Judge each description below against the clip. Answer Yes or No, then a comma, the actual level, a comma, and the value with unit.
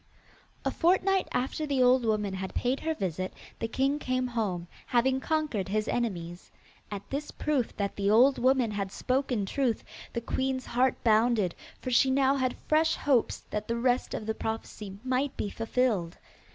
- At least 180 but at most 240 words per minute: No, average, 170 wpm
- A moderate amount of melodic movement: Yes, average, 4.0 semitones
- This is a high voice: Yes, high, 245 Hz